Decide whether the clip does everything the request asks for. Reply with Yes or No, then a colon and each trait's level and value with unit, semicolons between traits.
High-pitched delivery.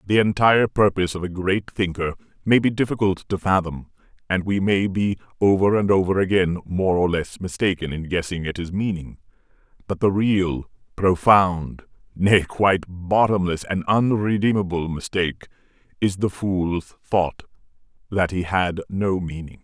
No: very low, 95 Hz